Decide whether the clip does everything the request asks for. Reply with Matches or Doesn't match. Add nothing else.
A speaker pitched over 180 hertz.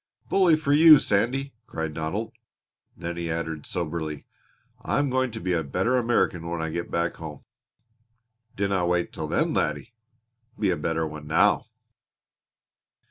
Doesn't match